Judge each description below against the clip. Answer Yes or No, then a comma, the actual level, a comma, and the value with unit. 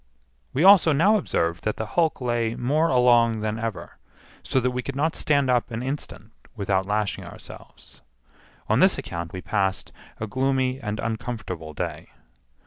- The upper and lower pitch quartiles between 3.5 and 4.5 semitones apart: Yes, average, 4.1 semitones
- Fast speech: No, average, 155 wpm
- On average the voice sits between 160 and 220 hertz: No, low, 120 Hz